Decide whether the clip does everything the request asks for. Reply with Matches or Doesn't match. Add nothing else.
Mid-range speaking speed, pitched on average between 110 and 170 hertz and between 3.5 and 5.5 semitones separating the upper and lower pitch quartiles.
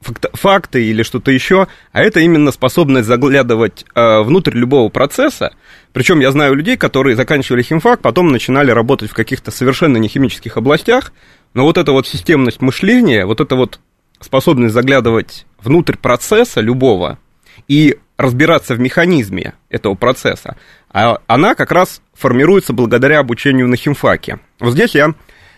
Matches